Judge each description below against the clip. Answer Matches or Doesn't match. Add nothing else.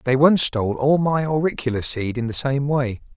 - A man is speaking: Matches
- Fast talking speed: Matches